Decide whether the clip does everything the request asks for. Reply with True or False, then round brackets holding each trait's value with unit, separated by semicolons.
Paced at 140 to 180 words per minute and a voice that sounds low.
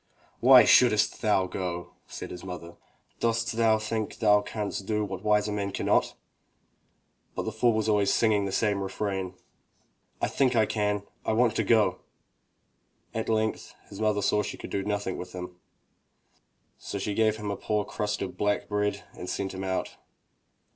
True (170 wpm; 105 Hz)